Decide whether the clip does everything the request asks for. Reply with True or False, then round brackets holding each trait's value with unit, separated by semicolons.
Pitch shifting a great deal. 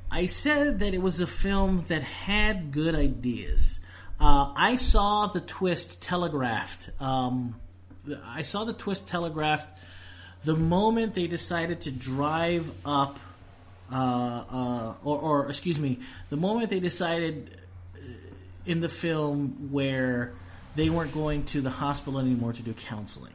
True (6.6 semitones)